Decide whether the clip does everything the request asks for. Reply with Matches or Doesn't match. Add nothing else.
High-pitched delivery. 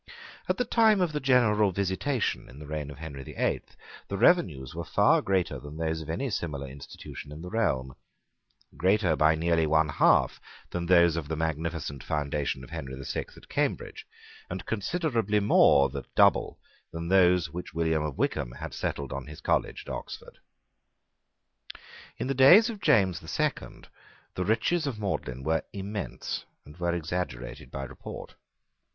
Doesn't match